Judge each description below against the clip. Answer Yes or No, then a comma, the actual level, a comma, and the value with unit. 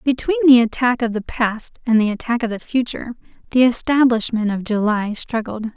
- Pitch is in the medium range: No, high, 230 Hz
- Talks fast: No, average, 175 wpm